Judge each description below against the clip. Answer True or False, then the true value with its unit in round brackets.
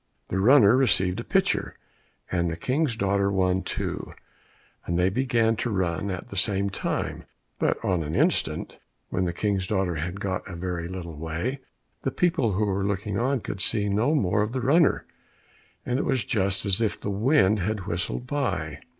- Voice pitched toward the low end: True (100 Hz)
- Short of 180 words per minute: False (185 wpm)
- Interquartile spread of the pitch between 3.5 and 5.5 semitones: True (4.2 semitones)